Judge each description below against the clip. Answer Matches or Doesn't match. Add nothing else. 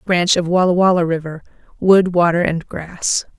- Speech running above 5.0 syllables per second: Doesn't match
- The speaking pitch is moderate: Matches